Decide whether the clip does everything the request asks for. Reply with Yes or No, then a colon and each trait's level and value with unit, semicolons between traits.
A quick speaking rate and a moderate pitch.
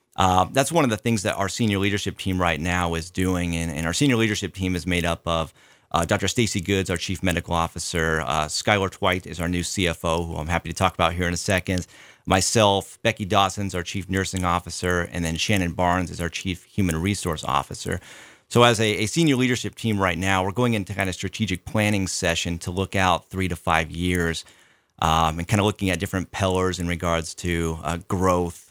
No: fast, 215 wpm; very low, 90 Hz